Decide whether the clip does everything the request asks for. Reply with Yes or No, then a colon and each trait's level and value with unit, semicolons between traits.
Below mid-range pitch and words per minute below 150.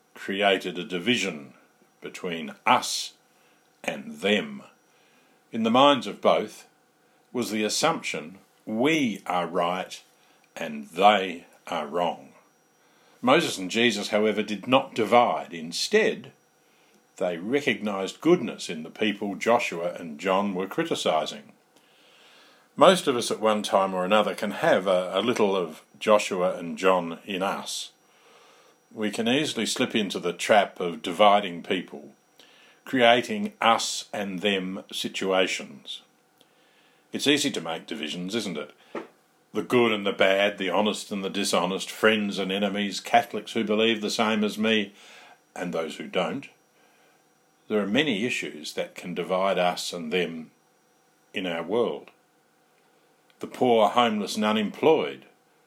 Yes: low, 110 Hz; slow, 135 wpm